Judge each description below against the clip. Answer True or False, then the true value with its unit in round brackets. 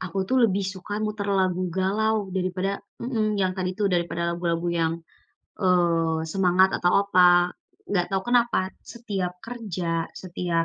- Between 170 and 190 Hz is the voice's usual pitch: True (185 Hz)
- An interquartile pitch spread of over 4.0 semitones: False (2.5 semitones)